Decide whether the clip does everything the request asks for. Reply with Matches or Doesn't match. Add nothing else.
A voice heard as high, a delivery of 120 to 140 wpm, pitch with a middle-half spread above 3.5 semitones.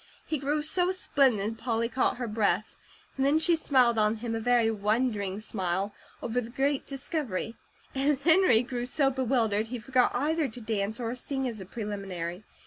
Doesn't match